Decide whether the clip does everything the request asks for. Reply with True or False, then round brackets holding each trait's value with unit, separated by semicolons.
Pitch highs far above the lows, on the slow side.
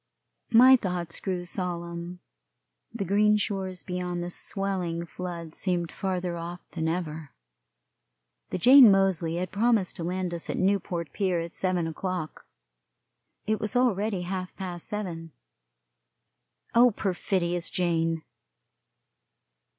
False (2.4 semitones; 120 wpm)